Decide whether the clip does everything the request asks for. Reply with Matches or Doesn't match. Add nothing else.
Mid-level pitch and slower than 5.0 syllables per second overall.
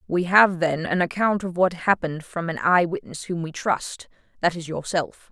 Matches